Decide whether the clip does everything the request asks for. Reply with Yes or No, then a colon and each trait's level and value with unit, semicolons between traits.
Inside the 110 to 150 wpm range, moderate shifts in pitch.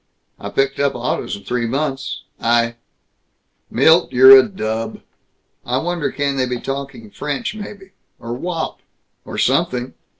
Yes: average, 140 wpm; average, 4.3 semitones